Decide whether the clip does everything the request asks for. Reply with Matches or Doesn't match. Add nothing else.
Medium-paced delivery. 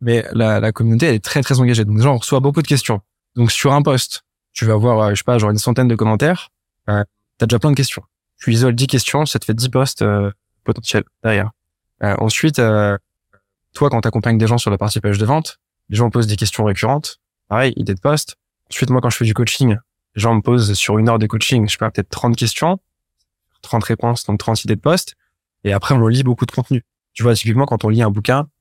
Doesn't match